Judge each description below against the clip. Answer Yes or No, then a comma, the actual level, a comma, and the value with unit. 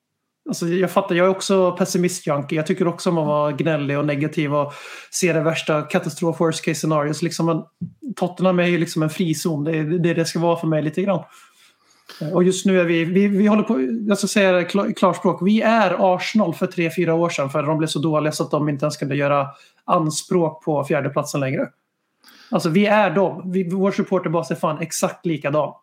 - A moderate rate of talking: No, fast, 205 wpm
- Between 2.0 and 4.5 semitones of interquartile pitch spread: Yes, average, 3.2 semitones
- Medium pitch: Yes, medium, 170 Hz